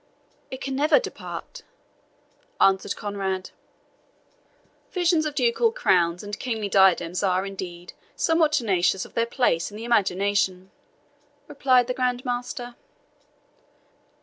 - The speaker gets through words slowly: Yes, slow, 115 wpm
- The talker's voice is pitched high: Yes, high, 215 Hz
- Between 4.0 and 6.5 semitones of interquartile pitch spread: Yes, average, 5.3 semitones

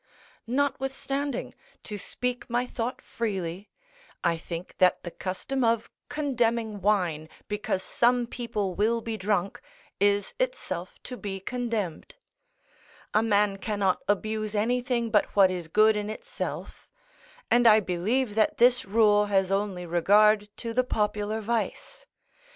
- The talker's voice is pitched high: Yes, high, 215 Hz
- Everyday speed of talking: No, slow, 130 wpm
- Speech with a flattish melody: No, average, 3.3 semitones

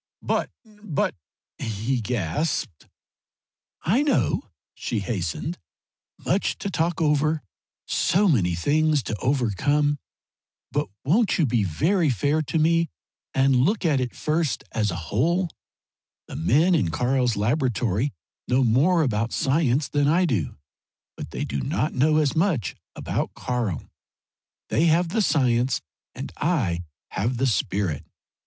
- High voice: No, low, 135 Hz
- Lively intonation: Yes, wide, 6.1 semitones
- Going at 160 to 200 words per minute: No, slow, 135 wpm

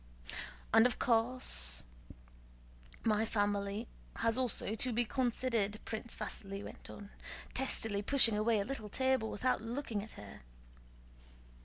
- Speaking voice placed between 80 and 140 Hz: No, high, 225 Hz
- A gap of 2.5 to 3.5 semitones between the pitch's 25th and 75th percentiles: Yes, average, 3.1 semitones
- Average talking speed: No, slow, 130 wpm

